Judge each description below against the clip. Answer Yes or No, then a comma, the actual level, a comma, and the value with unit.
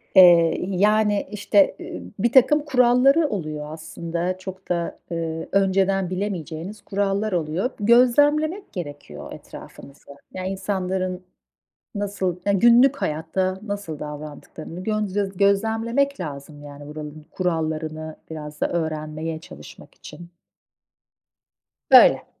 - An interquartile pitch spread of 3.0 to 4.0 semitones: No, average, 4.6 semitones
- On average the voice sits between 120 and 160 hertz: No, medium, 185 Hz